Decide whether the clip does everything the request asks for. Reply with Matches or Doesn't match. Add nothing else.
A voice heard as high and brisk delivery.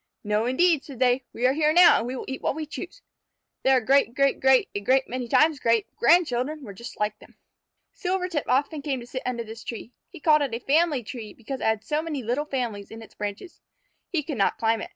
Matches